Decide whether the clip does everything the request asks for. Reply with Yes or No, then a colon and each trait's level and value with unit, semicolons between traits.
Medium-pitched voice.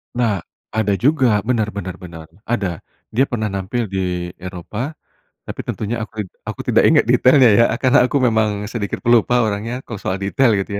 No: low, 110 Hz